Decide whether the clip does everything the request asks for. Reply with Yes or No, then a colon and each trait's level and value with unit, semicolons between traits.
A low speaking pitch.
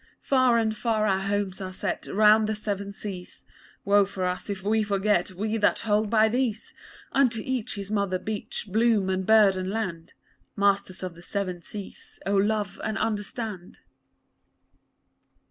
No: high, 205 Hz